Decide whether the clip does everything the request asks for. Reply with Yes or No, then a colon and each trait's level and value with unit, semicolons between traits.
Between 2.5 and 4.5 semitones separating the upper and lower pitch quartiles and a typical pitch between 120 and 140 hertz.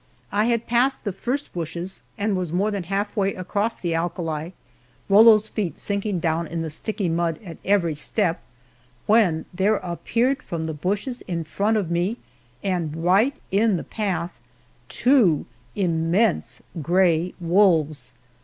No: average, 4.1 semitones; medium, 185 Hz